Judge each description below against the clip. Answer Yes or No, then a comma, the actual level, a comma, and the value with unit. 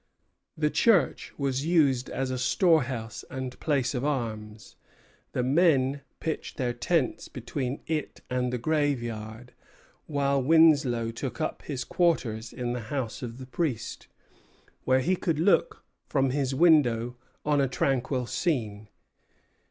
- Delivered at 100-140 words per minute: Yes, slow, 135 wpm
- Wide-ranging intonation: No, average, 3.6 semitones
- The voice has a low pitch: Yes, low, 130 Hz